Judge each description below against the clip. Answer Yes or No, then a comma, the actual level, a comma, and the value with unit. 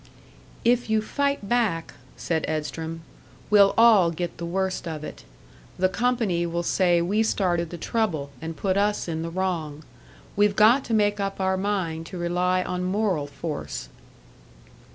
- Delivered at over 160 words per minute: No, average, 155 wpm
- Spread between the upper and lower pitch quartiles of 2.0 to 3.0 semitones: No, average, 3.8 semitones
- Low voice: No, medium, 185 Hz